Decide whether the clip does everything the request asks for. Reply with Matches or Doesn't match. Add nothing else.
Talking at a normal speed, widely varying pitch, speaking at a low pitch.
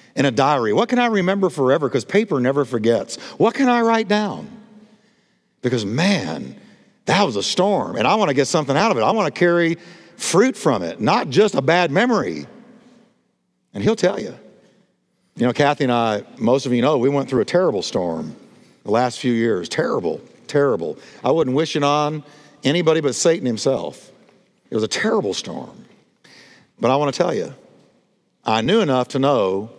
Doesn't match